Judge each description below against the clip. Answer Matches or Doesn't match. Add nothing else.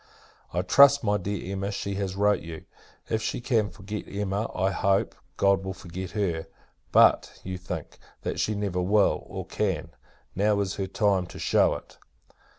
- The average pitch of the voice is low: Matches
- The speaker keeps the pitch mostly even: Matches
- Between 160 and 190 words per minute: Matches